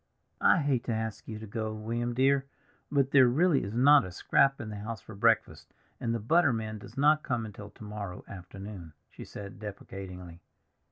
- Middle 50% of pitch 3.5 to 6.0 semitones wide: Yes, average, 4.3 semitones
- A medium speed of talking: Yes, average, 190 wpm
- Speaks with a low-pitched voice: Yes, low, 110 Hz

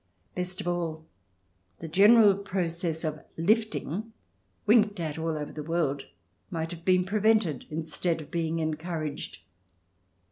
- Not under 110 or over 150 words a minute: Yes, average, 140 wpm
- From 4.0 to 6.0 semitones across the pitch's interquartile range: No, average, 3.3 semitones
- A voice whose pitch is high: No, medium, 170 Hz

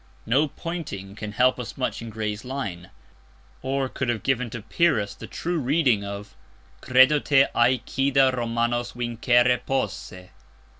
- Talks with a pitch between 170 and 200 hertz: No, low, 120 Hz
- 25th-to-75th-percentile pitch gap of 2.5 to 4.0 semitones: Yes, average, 3.6 semitones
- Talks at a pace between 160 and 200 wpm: No, average, 140 wpm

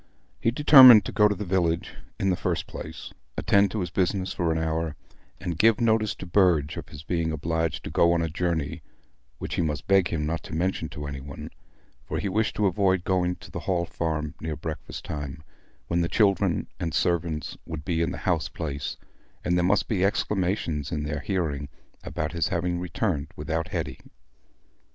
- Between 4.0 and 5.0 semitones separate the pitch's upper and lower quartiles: No, average, 3.1 semitones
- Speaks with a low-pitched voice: Yes, very low, 85 Hz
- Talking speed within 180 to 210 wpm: Yes, average, 195 wpm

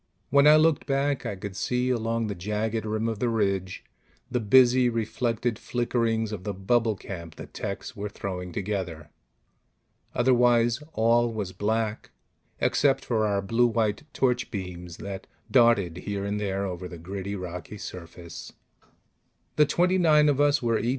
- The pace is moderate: Yes, average, 155 wpm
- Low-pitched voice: Yes, low, 110 Hz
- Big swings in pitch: No, average, 3.8 semitones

